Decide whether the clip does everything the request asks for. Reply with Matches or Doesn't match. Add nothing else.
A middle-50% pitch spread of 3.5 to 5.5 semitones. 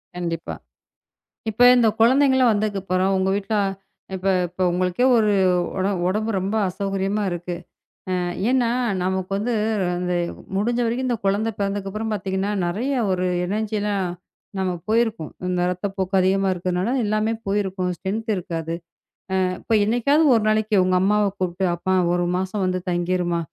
Doesn't match